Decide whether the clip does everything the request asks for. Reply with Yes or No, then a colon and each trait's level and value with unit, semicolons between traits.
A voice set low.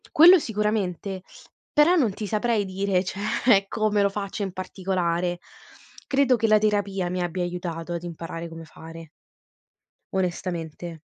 No: high, 190 Hz